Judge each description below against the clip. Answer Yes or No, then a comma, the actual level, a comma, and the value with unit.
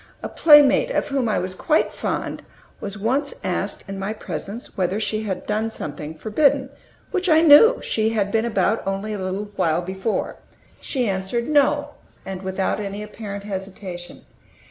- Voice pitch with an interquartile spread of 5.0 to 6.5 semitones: Yes, wide, 5.5 semitones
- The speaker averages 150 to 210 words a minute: Yes, average, 165 wpm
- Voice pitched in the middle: No, high, 210 Hz